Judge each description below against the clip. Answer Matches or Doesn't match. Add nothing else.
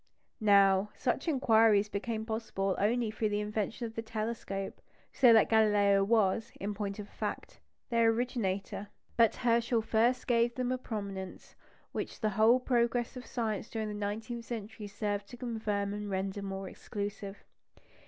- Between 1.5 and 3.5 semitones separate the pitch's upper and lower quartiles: Matches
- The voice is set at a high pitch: Matches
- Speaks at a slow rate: Doesn't match